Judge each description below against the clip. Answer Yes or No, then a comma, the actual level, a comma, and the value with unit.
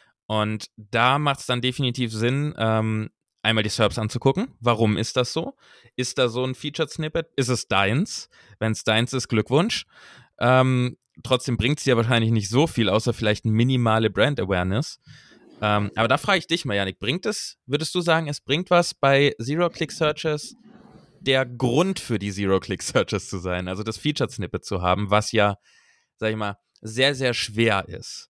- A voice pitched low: Yes, low, 120 Hz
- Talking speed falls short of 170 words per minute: No, average, 180 wpm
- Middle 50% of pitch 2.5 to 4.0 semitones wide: No, average, 4.8 semitones